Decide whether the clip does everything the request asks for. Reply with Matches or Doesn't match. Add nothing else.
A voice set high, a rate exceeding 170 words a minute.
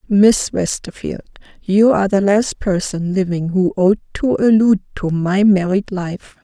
Doesn't match